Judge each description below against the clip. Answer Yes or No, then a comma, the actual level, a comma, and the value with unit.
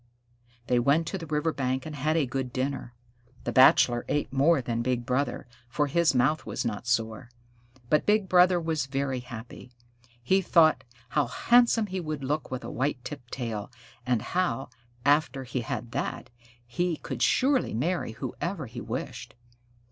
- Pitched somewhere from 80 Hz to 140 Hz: Yes, low, 135 Hz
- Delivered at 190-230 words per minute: No, average, 165 wpm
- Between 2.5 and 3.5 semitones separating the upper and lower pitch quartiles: No, average, 4.8 semitones